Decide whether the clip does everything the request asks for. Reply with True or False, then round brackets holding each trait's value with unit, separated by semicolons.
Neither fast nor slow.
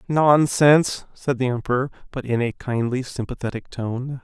False (125 wpm)